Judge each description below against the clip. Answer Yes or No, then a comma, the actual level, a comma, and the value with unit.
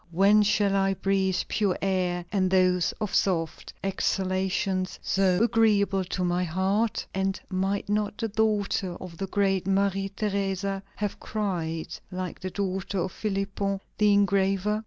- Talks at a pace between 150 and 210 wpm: No, slow, 135 wpm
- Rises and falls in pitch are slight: Yes, narrow, 1.4 semitones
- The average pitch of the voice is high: Yes, high, 195 Hz